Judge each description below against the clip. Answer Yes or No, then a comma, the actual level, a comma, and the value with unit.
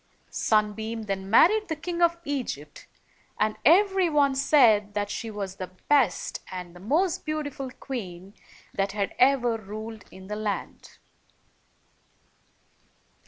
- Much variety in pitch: Yes, wide, 6.3 semitones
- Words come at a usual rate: No, slow, 120 wpm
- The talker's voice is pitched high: Yes, high, 225 Hz